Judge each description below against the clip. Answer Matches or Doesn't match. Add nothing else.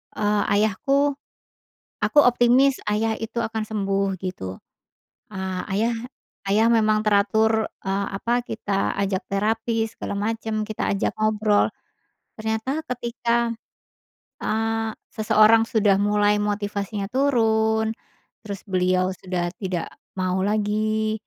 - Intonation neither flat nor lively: Doesn't match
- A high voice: Matches